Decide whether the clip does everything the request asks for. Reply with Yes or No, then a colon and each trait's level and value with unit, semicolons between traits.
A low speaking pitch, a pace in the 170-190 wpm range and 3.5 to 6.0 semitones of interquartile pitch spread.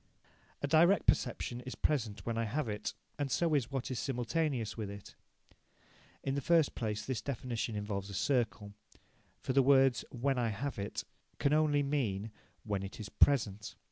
Yes: low, 125 Hz; average, 175 wpm; average, 4.9 semitones